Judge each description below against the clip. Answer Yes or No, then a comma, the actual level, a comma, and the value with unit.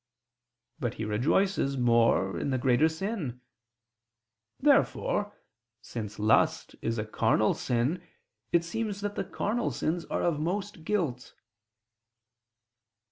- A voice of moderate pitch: Yes, medium, 150 Hz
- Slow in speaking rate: Yes, slow, 115 wpm